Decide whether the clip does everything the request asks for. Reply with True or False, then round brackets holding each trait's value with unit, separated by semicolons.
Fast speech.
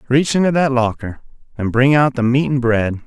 True (215 wpm)